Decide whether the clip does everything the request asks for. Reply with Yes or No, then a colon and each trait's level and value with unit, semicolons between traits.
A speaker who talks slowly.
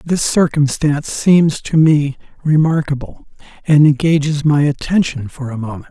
Yes: slow, 130 wpm